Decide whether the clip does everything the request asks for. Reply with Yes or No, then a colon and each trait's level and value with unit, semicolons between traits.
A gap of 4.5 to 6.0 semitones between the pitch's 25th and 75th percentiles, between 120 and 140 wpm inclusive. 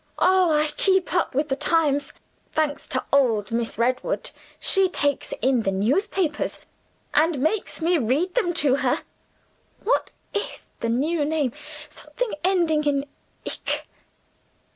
Yes: average, 4.9 semitones; slow, 135 wpm